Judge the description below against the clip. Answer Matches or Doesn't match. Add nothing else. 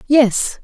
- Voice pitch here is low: Doesn't match